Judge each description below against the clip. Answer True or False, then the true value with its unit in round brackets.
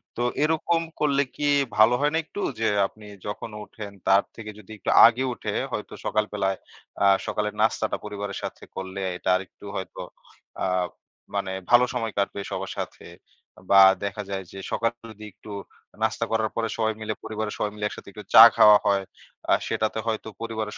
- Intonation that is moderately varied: False (2.0 semitones)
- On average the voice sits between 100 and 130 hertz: True (110 Hz)